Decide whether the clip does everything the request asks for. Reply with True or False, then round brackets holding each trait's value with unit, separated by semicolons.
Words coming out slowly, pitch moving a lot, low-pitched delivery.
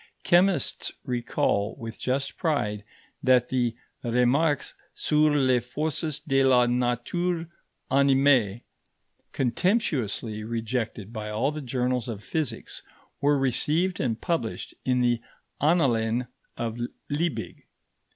False (105 wpm; 4.0 semitones; 130 Hz)